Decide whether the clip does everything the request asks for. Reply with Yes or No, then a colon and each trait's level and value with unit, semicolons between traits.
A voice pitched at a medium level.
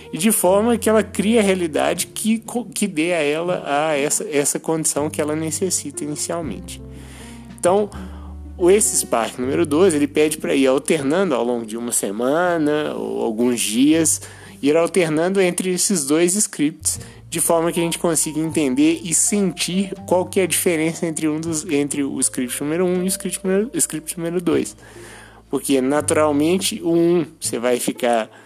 Yes: medium, 160 Hz